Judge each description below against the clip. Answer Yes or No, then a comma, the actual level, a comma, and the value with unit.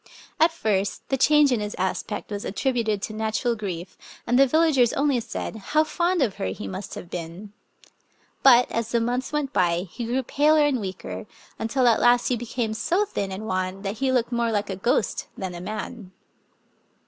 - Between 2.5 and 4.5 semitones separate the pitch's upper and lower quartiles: No, average, 5.0 semitones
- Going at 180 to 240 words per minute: Yes, average, 195 wpm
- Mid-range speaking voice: No, high, 230 Hz